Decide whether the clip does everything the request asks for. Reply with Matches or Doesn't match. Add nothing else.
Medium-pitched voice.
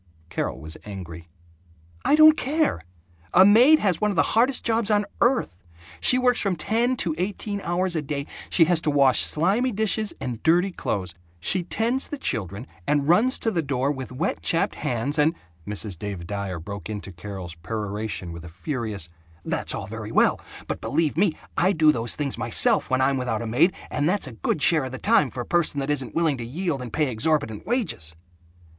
Matches